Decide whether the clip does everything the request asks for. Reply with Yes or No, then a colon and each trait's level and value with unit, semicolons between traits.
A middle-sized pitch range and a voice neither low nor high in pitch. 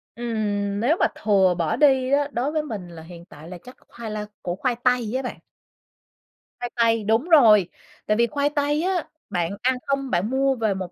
No: average, 5.0 semitones; high, 230 Hz